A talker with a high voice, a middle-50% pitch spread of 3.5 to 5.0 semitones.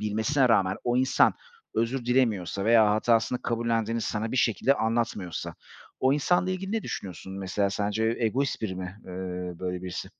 No: low, 115 Hz; average, 3.9 semitones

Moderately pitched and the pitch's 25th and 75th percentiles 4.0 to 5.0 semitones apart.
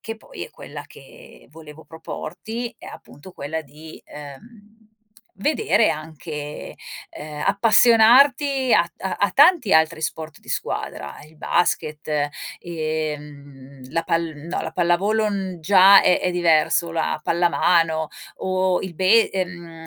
Yes: medium, 170 Hz; average, 4.6 semitones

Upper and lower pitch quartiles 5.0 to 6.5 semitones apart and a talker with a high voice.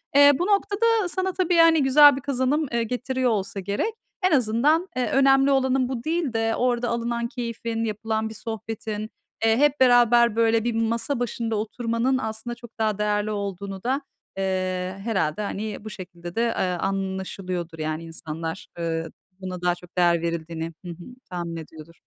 Yes: wide, 5.4 semitones; high, 225 Hz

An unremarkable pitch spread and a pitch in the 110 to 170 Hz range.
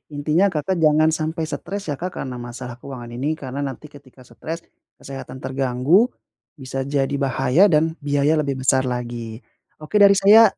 Yes: average, 3.6 semitones; medium, 140 Hz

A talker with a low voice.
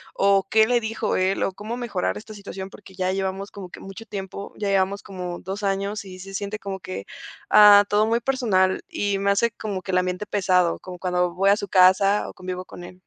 No: high, 195 Hz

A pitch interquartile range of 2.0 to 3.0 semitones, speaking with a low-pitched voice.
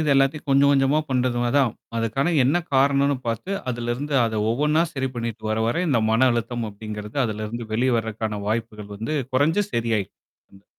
No: average, 3.7 semitones; low, 120 Hz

